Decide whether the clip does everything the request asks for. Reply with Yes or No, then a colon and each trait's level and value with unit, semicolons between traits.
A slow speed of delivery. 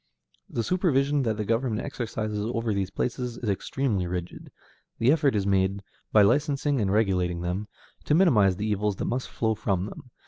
No: average, 175 wpm